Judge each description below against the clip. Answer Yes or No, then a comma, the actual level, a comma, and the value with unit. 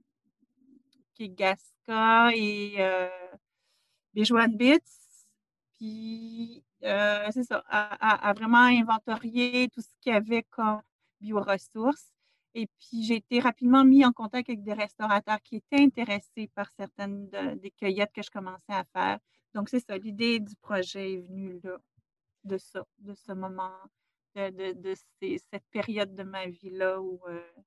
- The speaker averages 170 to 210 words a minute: No, average, 155 wpm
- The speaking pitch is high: Yes, high, 210 Hz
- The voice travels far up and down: No, average, 3.2 semitones